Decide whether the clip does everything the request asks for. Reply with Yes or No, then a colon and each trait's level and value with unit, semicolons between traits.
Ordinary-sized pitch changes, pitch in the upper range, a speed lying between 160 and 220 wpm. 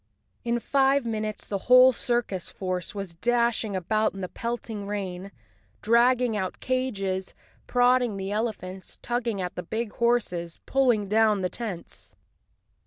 No: average, 3.9 semitones; high, 215 Hz; slow, 135 wpm